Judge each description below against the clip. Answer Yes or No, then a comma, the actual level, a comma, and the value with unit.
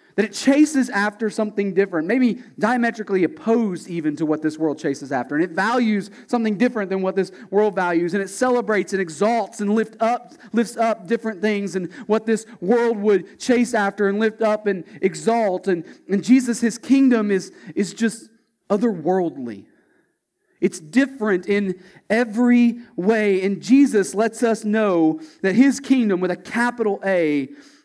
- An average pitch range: Yes, average, 3.6 semitones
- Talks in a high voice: Yes, high, 210 Hz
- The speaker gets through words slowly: No, average, 165 wpm